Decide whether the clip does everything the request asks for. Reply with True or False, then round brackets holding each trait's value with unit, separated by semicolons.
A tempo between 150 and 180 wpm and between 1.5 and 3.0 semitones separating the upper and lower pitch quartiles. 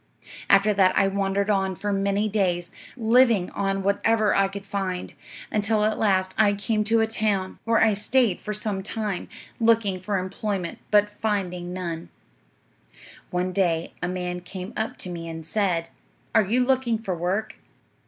True (165 wpm; 2.7 semitones)